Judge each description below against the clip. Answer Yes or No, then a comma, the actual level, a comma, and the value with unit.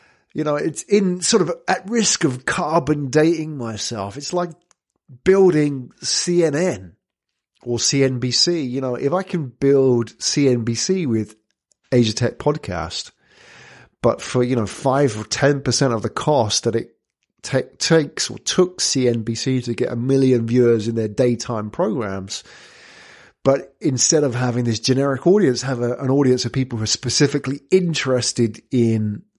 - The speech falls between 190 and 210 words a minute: No, average, 150 wpm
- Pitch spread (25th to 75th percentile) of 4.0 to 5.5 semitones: Yes, average, 4.5 semitones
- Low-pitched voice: Yes, low, 130 Hz